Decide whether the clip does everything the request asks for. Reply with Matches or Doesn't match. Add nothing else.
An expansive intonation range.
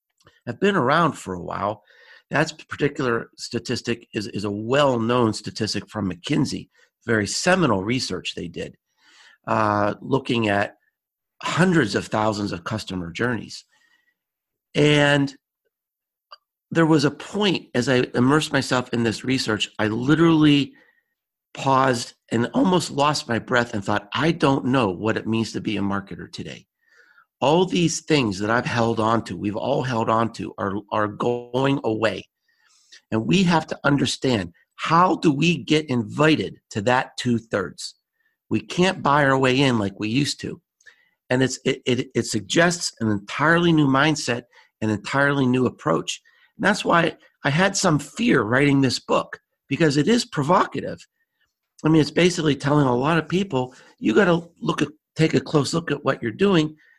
Matches